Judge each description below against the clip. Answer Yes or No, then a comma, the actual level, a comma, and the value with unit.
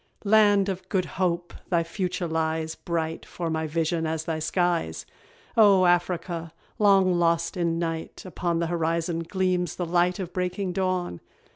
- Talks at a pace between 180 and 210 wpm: No, average, 150 wpm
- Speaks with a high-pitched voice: No, medium, 175 Hz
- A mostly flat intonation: Yes, narrow, 1.9 semitones